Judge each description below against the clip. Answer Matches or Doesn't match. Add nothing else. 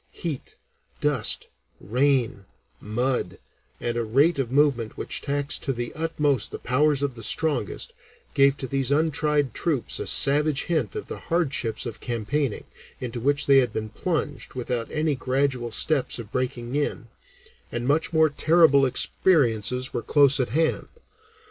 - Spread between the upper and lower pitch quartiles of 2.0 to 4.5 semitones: Matches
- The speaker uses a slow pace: Doesn't match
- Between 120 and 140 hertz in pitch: Matches